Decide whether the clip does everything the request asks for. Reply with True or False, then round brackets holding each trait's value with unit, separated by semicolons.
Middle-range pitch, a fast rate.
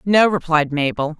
False (165 Hz; 150 wpm)